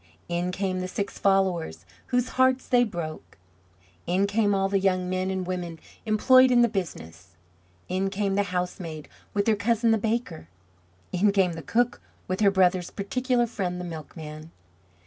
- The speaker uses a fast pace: No, average, 165 wpm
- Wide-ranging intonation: No, average, 3.3 semitones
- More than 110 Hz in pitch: Yes, high, 190 Hz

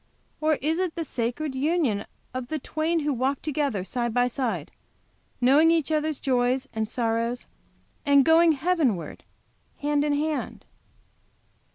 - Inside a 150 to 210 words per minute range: No, average, 140 wpm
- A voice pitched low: No, very high, 280 Hz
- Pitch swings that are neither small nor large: Yes, average, 4.1 semitones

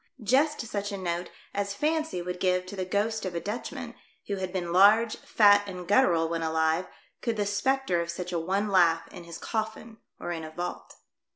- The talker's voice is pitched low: No, high, 190 Hz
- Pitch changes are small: No, average, 3.7 semitones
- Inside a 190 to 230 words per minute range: Yes, average, 200 wpm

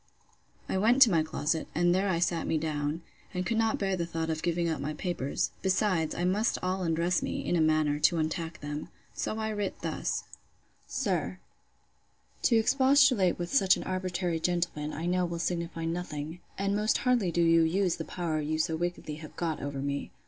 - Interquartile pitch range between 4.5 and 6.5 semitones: No, average, 2.9 semitones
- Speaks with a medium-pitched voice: Yes, medium, 170 Hz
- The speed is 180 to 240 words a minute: Yes, average, 195 wpm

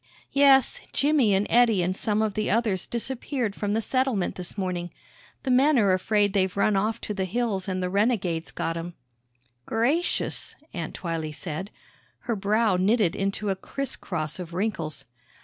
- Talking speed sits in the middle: Yes, average, 165 wpm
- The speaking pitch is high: Yes, high, 205 Hz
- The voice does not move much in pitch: No, average, 4.1 semitones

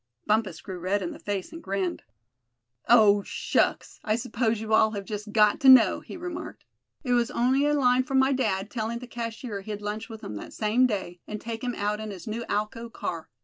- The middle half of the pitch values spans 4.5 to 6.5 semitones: No, average, 3.1 semitones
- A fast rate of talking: Yes, fast, 215 wpm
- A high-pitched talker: Yes, high, 220 Hz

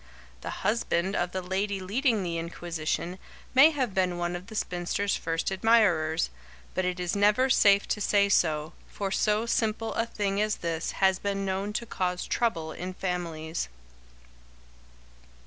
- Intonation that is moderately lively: Yes, average, 3.1 semitones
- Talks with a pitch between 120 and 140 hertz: No, high, 190 Hz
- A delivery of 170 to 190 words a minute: No, average, 155 wpm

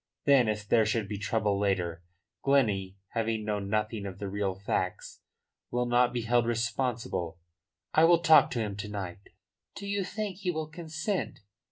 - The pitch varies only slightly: No, wide, 5.4 semitones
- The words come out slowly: No, average, 170 wpm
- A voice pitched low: Yes, low, 110 Hz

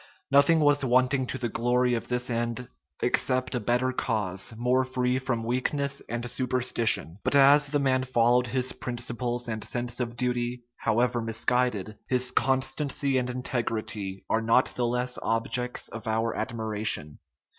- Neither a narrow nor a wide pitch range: No, narrow, 1.8 semitones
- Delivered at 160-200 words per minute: No, average, 150 wpm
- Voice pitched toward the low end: Yes, low, 125 Hz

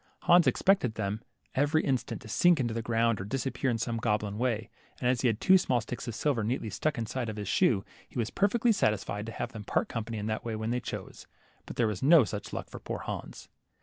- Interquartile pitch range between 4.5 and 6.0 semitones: No, average, 3.5 semitones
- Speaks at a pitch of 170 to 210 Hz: No, low, 115 Hz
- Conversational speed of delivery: No, fast, 245 wpm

